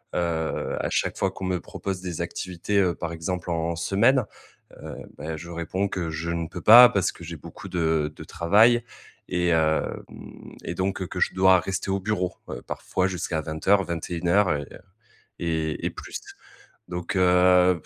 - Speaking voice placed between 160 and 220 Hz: No, very low, 90 Hz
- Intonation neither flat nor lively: No, narrow, 2.2 semitones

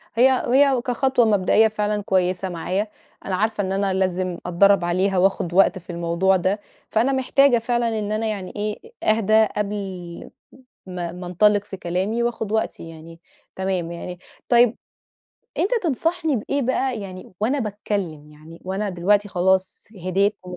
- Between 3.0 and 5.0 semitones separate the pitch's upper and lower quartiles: Yes, average, 3.4 semitones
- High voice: Yes, high, 200 Hz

